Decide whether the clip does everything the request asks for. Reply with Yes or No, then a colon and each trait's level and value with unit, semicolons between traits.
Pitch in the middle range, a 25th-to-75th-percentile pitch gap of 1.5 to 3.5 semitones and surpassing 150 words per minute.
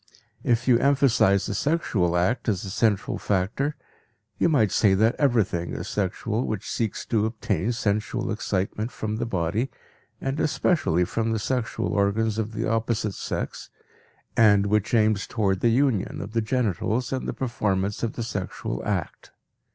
No: low, 110 Hz; average, 3.1 semitones; average, 160 wpm